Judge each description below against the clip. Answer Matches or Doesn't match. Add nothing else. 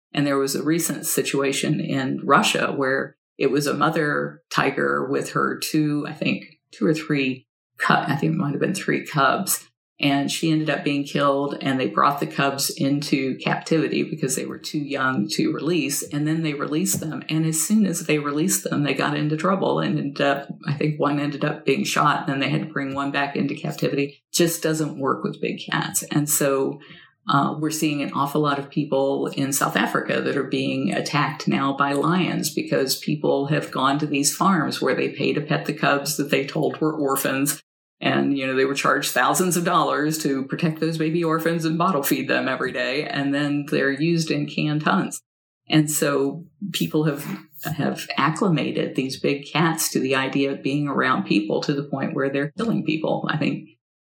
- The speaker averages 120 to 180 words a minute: Doesn't match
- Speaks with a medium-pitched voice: Matches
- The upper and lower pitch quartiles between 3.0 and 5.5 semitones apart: Doesn't match